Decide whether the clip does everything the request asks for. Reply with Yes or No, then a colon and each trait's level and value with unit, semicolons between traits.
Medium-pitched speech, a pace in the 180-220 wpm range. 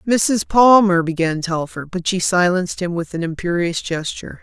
No: medium, 180 Hz; average, 165 wpm